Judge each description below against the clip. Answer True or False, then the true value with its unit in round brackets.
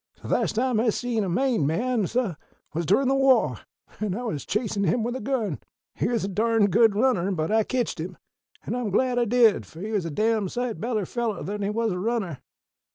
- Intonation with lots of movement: False (3.7 semitones)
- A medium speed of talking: False (225 wpm)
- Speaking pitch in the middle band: False (220 Hz)